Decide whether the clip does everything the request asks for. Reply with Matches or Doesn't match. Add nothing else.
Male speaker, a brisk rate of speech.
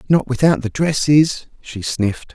Doesn't match